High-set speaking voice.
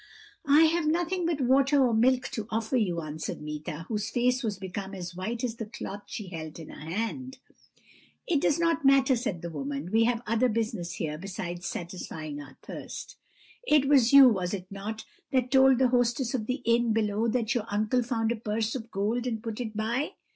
Yes: high, 225 Hz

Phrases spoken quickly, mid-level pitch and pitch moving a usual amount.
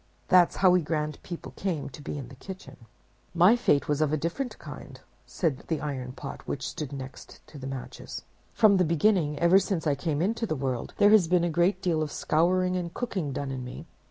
Yes: fast, 215 wpm; medium, 165 Hz; average, 4.3 semitones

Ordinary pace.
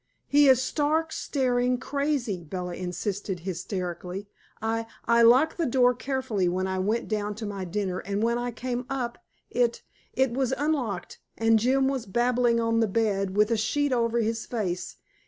Yes: average, 170 wpm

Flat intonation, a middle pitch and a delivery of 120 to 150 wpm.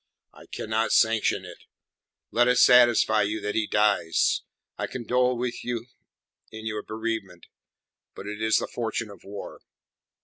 No: narrow, 2.3 semitones; low, 110 Hz; average, 145 wpm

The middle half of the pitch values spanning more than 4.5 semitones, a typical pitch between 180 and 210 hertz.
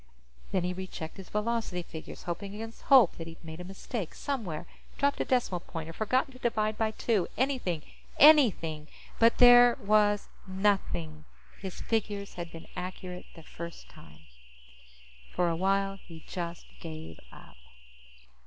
Yes: average, 4.9 semitones; high, 190 Hz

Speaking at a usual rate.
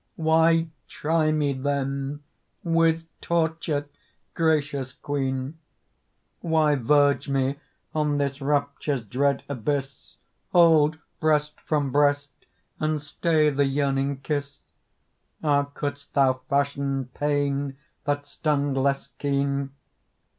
No: slow, 100 wpm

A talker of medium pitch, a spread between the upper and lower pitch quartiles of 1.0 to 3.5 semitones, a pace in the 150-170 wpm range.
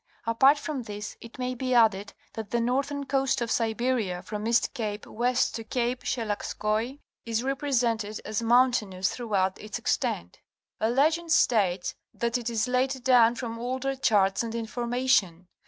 No: high, 235 Hz; average, 3.0 semitones; average, 155 wpm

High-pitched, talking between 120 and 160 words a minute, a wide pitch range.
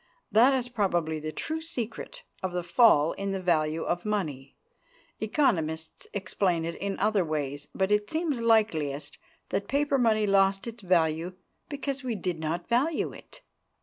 Yes: high, 195 Hz; average, 155 wpm; wide, 6.3 semitones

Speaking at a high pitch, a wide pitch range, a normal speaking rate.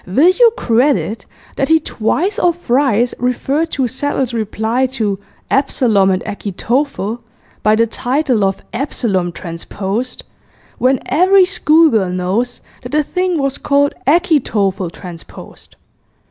No: very high, 250 Hz; wide, 5.9 semitones; slow, 120 wpm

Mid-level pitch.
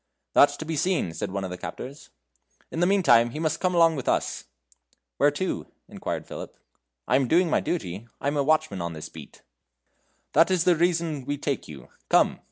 Yes: medium, 145 Hz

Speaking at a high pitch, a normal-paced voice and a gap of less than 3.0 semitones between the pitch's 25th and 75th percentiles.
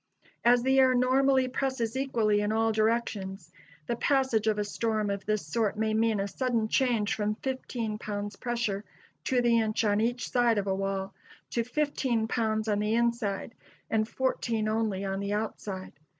Yes: high, 220 Hz; average, 175 wpm; narrow, 2.6 semitones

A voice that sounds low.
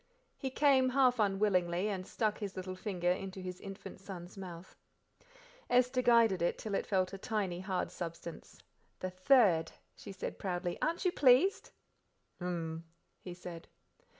No: high, 190 Hz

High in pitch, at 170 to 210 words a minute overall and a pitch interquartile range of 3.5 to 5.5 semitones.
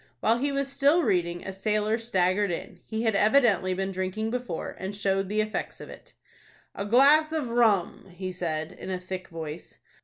Yes: high, 205 Hz; average, 185 wpm; average, 4.2 semitones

